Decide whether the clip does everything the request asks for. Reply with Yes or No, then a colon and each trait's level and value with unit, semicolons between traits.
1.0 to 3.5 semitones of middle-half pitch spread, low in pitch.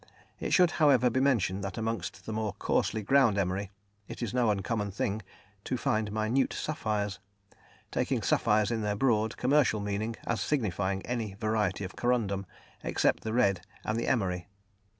Yes: average, 3.2 semitones; low, 110 Hz